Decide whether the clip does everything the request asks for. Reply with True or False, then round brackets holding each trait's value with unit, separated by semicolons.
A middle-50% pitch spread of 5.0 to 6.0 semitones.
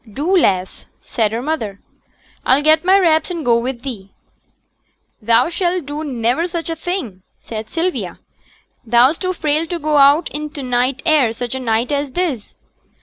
True (5.5 semitones)